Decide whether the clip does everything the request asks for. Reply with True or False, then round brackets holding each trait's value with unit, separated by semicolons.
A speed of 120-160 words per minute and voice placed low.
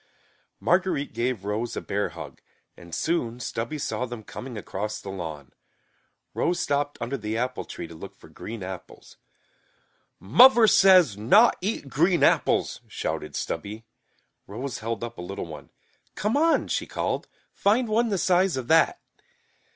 True (150 wpm; 125 Hz)